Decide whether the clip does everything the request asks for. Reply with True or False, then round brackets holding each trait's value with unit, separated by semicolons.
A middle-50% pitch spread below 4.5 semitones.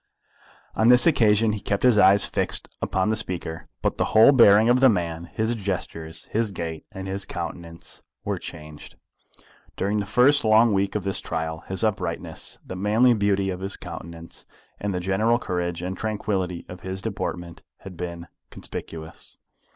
True (3.8 semitones)